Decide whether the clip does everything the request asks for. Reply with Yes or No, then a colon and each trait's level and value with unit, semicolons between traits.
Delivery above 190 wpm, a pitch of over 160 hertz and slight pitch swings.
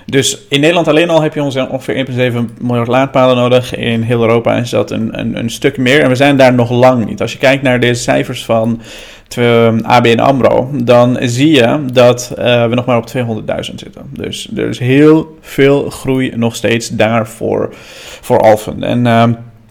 No: fast, 200 wpm; low, 125 Hz; narrow, 2.3 semitones